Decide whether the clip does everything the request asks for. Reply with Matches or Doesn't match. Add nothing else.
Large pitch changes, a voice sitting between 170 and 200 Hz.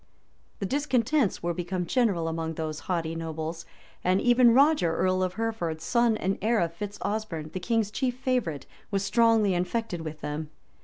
Matches